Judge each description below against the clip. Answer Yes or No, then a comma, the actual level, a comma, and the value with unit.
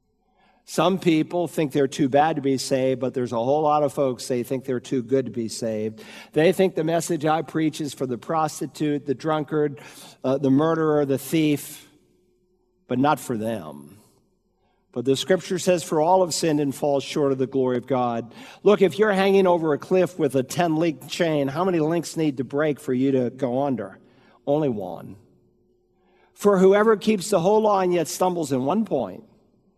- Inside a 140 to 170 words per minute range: No, average, 195 wpm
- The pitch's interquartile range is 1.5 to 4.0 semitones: No, average, 4.8 semitones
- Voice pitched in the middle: Yes, medium, 150 Hz